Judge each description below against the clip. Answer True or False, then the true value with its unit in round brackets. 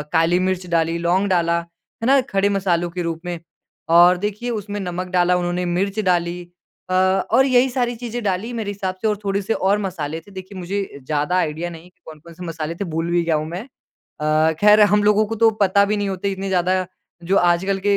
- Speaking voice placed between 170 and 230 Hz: True (185 Hz)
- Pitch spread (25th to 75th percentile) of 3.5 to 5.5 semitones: False (3.0 semitones)